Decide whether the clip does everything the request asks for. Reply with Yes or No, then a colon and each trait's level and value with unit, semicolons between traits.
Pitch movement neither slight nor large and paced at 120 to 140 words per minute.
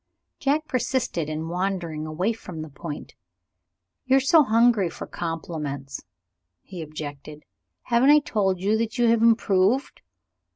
No: wide, 6.9 semitones; slow, 135 wpm